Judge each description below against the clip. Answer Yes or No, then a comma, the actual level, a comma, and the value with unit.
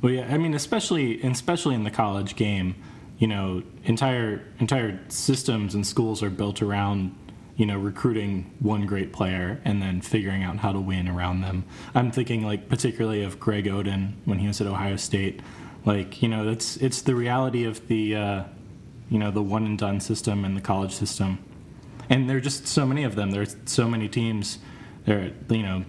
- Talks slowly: No, average, 195 wpm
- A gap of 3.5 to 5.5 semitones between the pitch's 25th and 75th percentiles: Yes, average, 3.8 semitones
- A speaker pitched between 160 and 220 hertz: No, low, 105 Hz